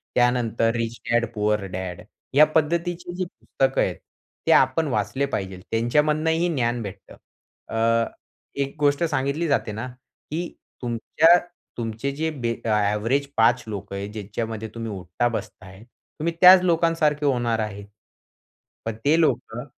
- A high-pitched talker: No, low, 120 Hz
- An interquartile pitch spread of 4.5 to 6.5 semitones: Yes, wide, 5.4 semitones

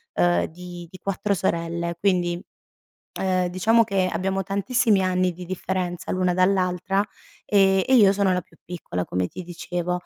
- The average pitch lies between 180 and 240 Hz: Yes, medium, 185 Hz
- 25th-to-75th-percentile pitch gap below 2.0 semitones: Yes, narrow, 1.6 semitones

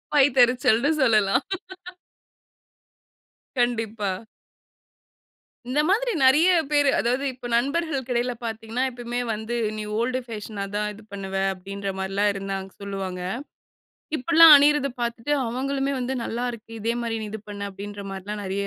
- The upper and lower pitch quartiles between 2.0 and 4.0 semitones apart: No, average, 4.5 semitones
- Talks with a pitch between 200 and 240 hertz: Yes, high, 235 Hz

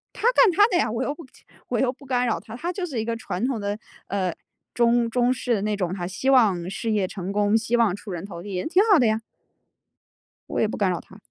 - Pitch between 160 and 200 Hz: No, high, 225 Hz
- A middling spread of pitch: Yes, average, 4.1 semitones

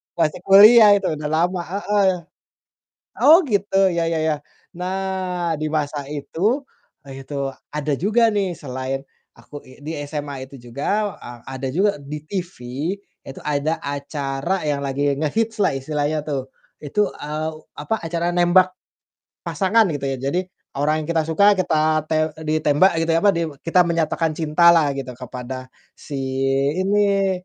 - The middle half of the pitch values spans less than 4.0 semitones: No, average, 4.9 semitones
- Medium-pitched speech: Yes, medium, 155 Hz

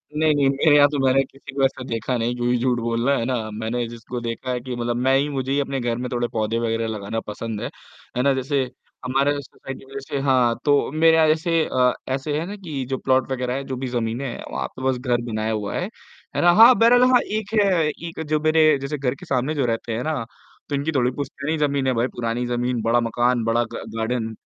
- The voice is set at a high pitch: No, low, 130 Hz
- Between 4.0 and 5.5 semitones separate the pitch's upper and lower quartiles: No, average, 3.2 semitones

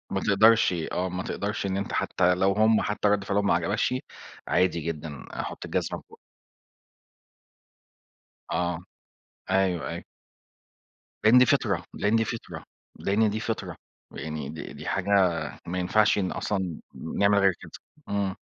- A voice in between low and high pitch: No, low, 100 Hz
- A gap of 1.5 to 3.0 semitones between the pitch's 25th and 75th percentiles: Yes, narrow, 2.6 semitones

